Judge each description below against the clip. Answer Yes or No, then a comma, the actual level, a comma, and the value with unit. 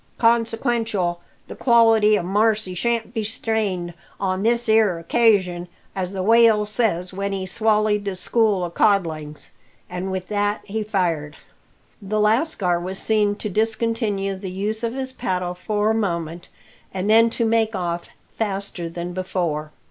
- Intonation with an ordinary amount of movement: Yes, average, 3.6 semitones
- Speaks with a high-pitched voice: Yes, high, 205 Hz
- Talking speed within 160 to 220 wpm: No, average, 150 wpm